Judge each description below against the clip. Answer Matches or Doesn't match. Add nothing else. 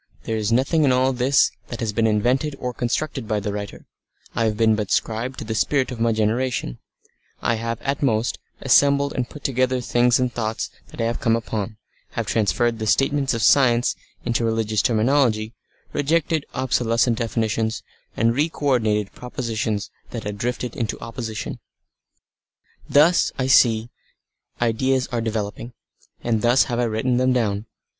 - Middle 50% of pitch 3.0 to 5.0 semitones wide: Doesn't match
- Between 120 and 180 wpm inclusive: Matches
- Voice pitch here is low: Matches